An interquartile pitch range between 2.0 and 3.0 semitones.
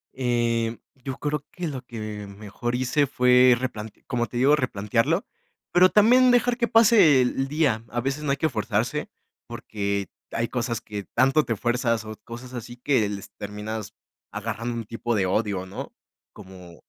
No: average, 4.0 semitones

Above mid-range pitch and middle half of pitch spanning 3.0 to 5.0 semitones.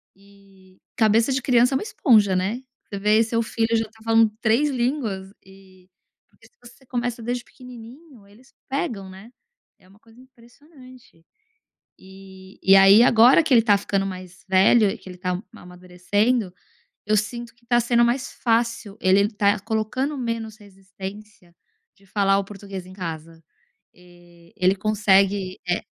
Yes: high, 210 Hz; average, 3.8 semitones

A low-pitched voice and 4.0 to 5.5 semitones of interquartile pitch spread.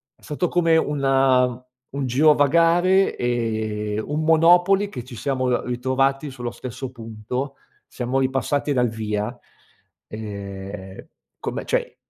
Yes: low, 130 Hz; average, 4.5 semitones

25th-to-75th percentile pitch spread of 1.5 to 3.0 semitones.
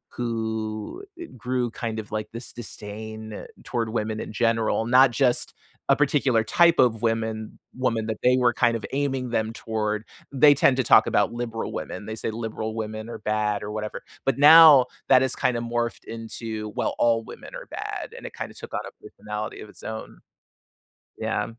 Yes: narrow, 2.4 semitones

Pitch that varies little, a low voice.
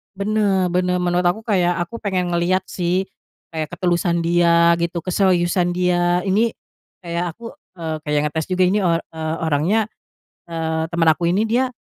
No: narrow, 1.9 semitones; medium, 175 Hz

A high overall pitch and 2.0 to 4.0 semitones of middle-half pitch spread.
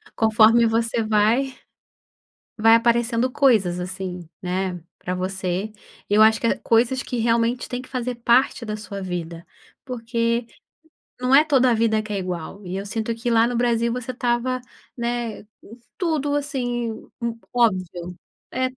Yes: high, 230 Hz; average, 3.4 semitones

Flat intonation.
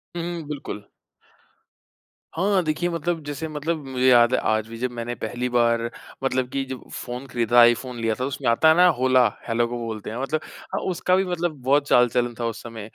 No: average, 4.4 semitones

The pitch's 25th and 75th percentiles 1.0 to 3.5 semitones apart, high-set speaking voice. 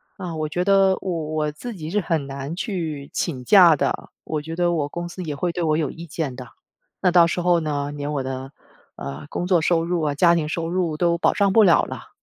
No: average, 3.1 semitones; medium, 165 Hz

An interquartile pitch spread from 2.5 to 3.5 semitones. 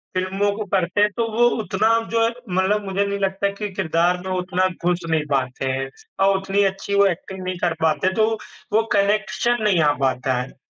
Yes: average, 2.8 semitones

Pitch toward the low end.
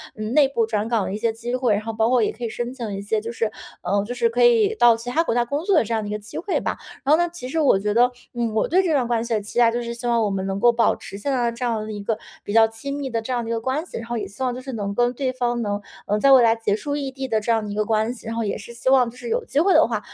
No: high, 235 Hz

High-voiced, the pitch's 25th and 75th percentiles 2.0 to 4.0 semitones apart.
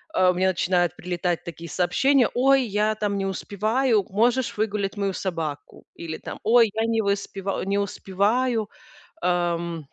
Yes: high, 200 Hz; average, 3.7 semitones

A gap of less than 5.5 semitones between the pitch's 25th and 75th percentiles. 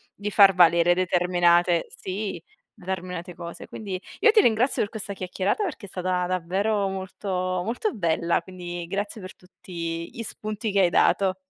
Yes: narrow, 2.6 semitones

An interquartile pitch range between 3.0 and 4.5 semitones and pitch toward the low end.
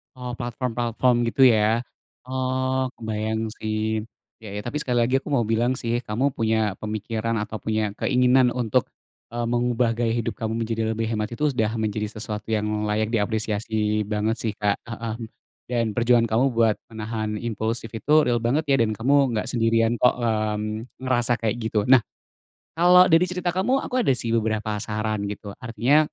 No: narrow, 2.4 semitones; low, 115 Hz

